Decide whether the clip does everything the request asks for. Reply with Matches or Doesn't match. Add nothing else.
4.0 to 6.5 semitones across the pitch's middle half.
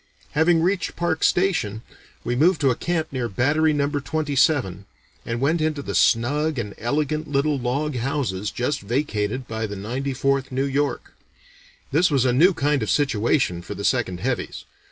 Matches